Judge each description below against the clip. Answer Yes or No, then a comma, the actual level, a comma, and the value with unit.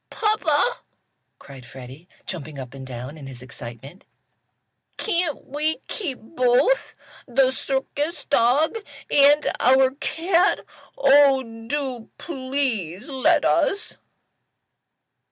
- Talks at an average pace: No, slow, 100 wpm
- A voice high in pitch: Yes, very high, 265 Hz